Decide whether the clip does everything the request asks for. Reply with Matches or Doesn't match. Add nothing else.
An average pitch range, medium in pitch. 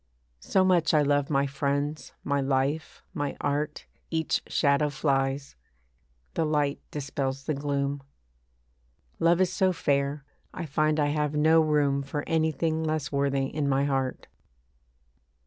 Doesn't match